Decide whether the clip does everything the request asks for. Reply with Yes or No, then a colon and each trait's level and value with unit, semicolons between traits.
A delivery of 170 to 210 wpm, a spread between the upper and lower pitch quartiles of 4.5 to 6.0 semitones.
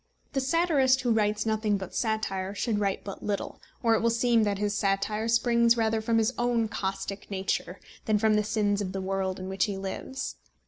No: average, 200 wpm; average, 2.8 semitones